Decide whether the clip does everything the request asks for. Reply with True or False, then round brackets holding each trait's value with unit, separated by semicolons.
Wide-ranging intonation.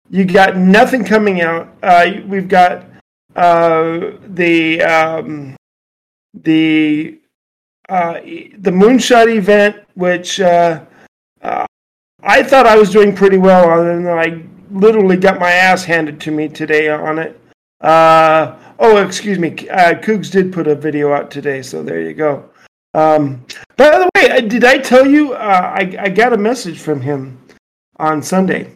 False (4.4 semitones)